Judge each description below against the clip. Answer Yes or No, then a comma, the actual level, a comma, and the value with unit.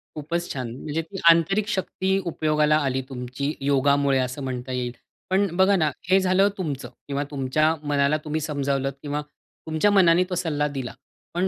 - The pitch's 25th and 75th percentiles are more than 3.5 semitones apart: Yes, average, 3.9 semitones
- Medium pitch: Yes, medium, 150 Hz